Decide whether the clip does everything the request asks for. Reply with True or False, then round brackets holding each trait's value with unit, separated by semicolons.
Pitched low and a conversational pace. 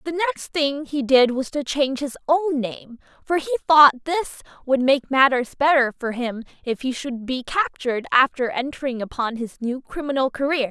False (270 Hz; 185 wpm)